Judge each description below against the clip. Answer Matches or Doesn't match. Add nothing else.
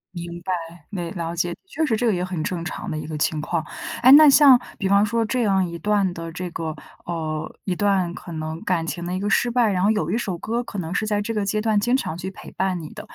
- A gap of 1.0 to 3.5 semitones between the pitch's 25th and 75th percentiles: Doesn't match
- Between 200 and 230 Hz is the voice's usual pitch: Doesn't match